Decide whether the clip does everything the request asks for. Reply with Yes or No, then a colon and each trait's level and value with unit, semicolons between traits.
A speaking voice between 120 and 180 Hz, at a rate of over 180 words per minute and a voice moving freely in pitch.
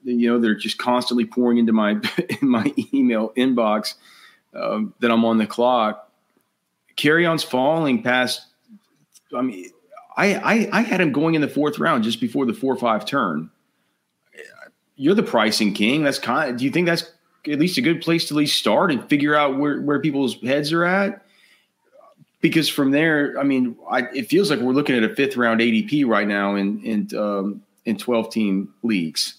Yes: low, 135 Hz; average, 195 wpm; wide, 6.0 semitones